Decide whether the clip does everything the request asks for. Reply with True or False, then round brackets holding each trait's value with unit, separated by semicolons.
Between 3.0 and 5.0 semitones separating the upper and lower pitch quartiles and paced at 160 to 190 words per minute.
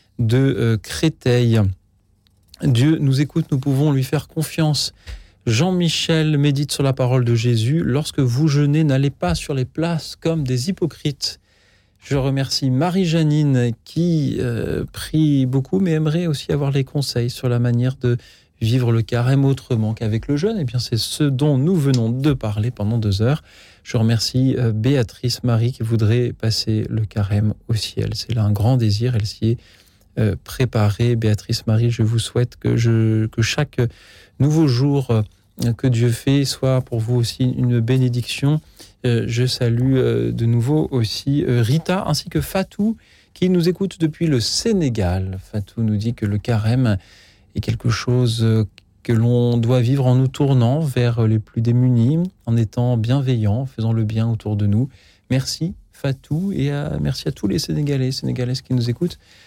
True (4.1 semitones; 165 wpm)